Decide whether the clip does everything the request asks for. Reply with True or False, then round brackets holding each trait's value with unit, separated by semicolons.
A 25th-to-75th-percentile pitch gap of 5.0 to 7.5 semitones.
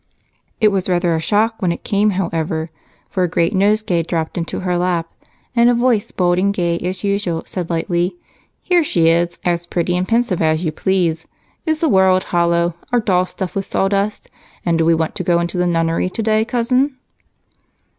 False (3.2 semitones)